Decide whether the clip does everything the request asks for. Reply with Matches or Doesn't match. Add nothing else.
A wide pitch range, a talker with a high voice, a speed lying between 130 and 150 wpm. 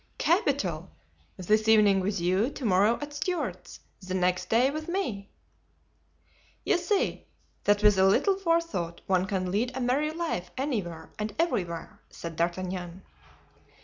Matches